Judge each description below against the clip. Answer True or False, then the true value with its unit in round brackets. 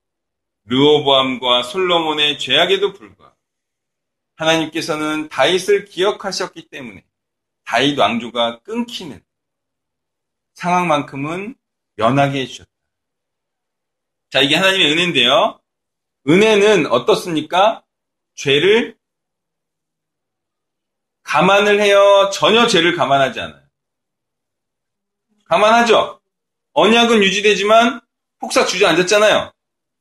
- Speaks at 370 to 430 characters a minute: False (225 characters per minute)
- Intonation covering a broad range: True (7.1 semitones)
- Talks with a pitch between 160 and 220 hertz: True (185 Hz)